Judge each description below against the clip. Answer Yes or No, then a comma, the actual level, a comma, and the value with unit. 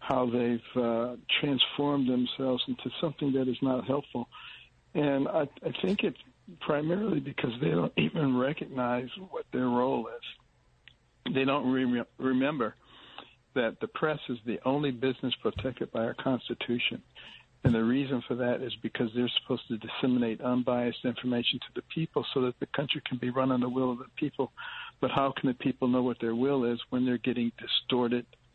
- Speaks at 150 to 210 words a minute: Yes, average, 175 wpm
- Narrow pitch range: Yes, narrow, 2.0 semitones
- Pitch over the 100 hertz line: Yes, low, 130 Hz